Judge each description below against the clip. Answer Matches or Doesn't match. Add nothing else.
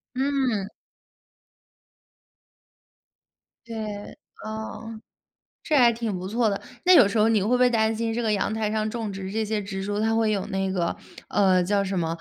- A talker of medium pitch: Doesn't match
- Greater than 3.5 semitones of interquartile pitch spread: Doesn't match